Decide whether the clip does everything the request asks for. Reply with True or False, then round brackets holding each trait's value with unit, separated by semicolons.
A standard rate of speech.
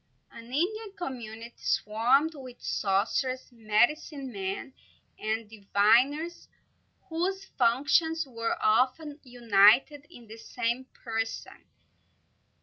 False (90 wpm)